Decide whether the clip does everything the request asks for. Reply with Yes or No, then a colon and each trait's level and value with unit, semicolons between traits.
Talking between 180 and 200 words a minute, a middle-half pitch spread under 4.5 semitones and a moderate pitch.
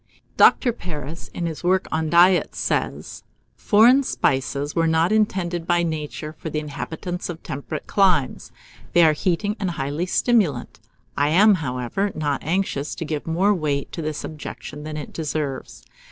No: average, 155 wpm; average, 3.6 semitones; medium, 160 Hz